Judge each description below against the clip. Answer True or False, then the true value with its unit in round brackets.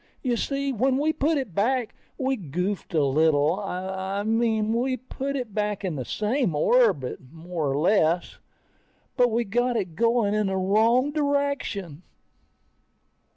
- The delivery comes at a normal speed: True (150 wpm)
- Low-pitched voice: False (215 Hz)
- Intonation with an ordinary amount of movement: False (6.0 semitones)